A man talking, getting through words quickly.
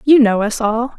No: female; fast, 245 wpm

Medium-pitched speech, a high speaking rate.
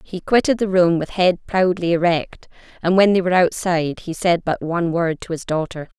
Yes: medium, 175 Hz; fast, 210 wpm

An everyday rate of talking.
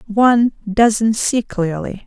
No: slow, 115 wpm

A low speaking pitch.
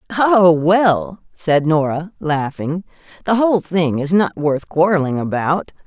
No: medium, 165 Hz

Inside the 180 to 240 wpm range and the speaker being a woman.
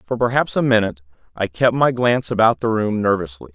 No: fast, 205 wpm; male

